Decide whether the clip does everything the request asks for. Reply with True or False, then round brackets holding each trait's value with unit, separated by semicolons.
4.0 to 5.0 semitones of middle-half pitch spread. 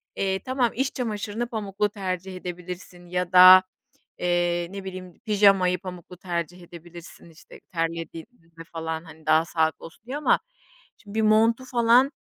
False (3.6 semitones)